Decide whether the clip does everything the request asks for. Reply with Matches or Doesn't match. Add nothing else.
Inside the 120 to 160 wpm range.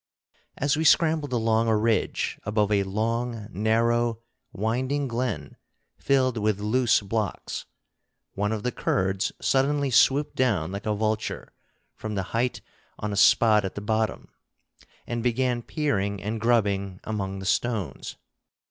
Matches